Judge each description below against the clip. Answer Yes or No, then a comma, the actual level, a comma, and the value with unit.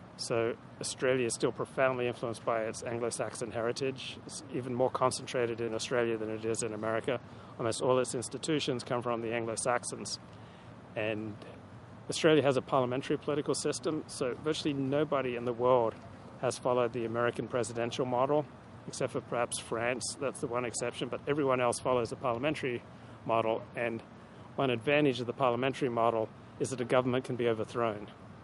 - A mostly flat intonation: Yes, narrow, 2.3 semitones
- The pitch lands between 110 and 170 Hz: Yes, low, 120 Hz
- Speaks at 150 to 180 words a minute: Yes, average, 160 wpm